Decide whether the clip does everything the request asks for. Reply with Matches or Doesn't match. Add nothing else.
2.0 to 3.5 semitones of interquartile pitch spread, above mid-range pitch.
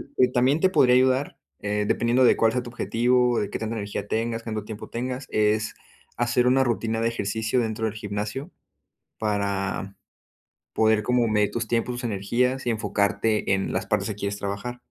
Doesn't match